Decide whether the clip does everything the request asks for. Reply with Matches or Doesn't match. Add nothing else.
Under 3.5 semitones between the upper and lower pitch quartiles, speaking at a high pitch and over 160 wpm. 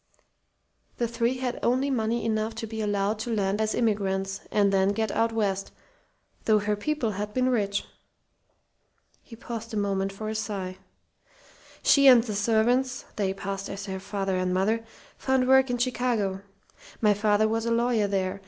Matches